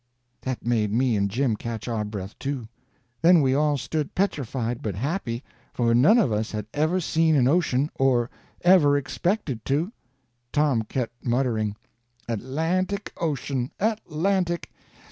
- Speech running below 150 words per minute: Yes, slow, 135 wpm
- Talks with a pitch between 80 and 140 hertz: Yes, low, 135 Hz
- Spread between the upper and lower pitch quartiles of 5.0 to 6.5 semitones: Yes, wide, 5.6 semitones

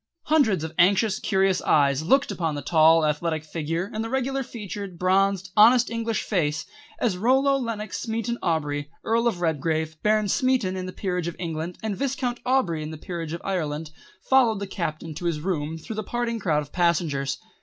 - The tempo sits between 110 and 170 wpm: No, average, 185 wpm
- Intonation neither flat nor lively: No, wide, 6.0 semitones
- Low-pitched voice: No, medium, 185 Hz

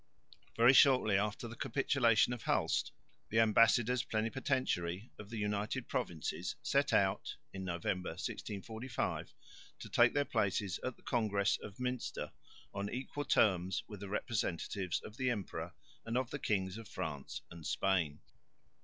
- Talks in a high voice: No, low, 105 Hz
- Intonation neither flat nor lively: Yes, average, 4.1 semitones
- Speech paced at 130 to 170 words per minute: Yes, average, 140 wpm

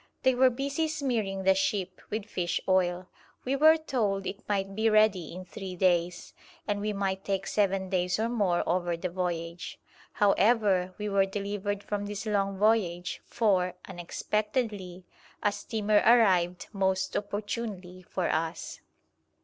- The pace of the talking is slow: No, average, 145 wpm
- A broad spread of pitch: No, average, 2.8 semitones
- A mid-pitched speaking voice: No, high, 195 Hz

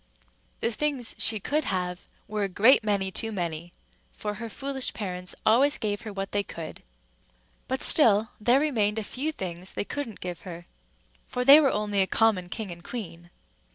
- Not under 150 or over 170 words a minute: No, average, 180 wpm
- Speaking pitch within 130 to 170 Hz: No, high, 210 Hz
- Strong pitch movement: No, average, 4.9 semitones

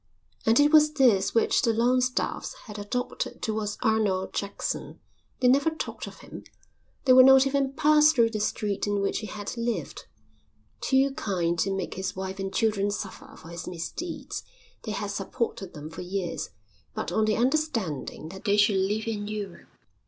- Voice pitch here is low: No, high, 215 Hz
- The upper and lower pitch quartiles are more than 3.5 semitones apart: Yes, average, 4.7 semitones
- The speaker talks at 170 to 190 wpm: Yes, average, 175 wpm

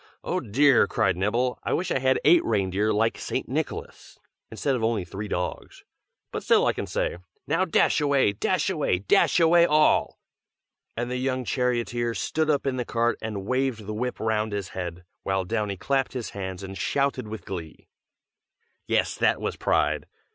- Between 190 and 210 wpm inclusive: No, average, 175 wpm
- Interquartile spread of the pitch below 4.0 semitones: No, average, 4.8 semitones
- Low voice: Yes, low, 115 Hz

